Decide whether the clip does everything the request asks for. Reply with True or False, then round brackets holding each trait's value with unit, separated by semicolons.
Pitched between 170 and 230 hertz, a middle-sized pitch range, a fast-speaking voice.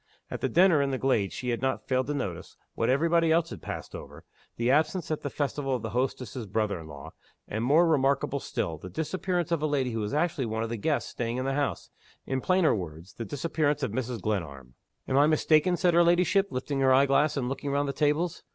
False (135 Hz; 5.0 semitones; 235 wpm)